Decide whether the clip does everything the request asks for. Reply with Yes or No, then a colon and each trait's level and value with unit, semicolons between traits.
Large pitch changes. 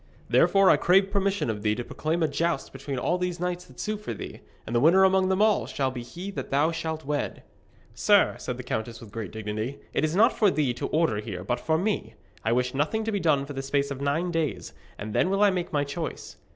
Yes: wide, 6.4 semitones